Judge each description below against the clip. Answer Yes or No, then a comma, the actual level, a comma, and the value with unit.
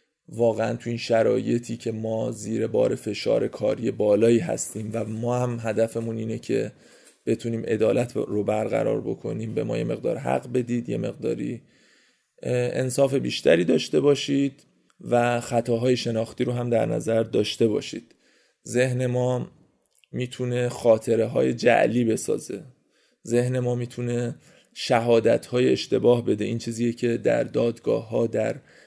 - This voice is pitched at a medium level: No, low, 120 Hz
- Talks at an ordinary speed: Yes, average, 135 wpm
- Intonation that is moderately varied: No, narrow, 1.6 semitones